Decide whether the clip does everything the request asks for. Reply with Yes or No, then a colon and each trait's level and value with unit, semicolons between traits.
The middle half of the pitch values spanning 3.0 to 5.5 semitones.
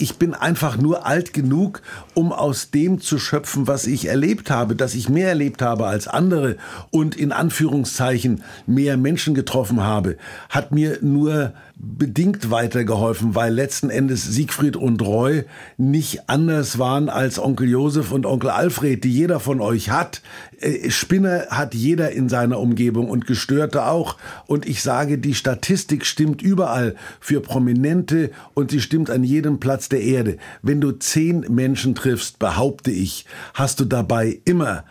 Yes: average, 3.6 semitones